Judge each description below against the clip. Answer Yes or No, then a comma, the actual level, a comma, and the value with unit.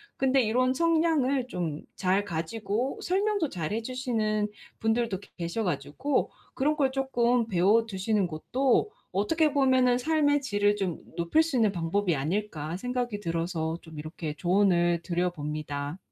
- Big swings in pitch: Yes, wide, 7.0 semitones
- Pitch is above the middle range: Yes, high, 210 Hz